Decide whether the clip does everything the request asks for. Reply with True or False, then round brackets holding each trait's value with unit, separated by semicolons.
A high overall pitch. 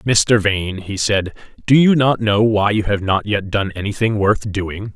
False (105 Hz)